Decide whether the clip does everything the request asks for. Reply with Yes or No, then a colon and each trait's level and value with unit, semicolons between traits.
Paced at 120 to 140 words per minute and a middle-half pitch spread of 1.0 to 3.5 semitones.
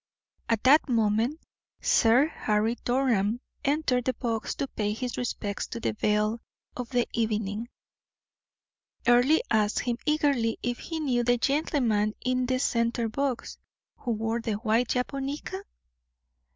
Yes: slow, 135 wpm; average, 2.8 semitones